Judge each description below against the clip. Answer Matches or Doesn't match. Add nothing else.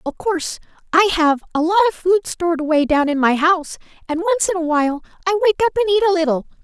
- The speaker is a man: Doesn't match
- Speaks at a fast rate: Matches